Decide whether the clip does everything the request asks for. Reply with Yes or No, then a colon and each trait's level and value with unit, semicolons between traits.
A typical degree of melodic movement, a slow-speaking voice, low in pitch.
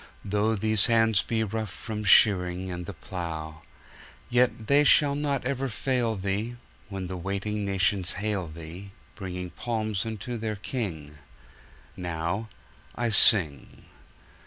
Yes: average, 3.7 semitones; slow, 115 wpm; low, 100 Hz